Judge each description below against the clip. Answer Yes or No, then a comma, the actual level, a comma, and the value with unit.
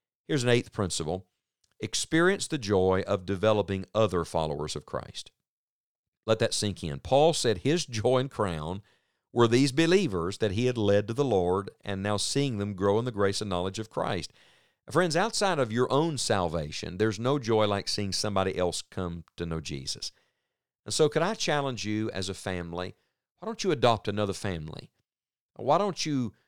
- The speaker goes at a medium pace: Yes, average, 185 wpm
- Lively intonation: Yes, wide, 6.1 semitones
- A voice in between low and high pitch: No, low, 105 Hz